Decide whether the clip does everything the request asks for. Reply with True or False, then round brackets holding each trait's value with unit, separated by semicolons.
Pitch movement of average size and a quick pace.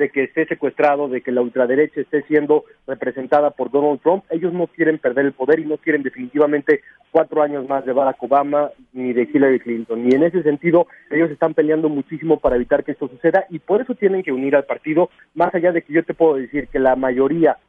True (3.2 semitones; 225 wpm)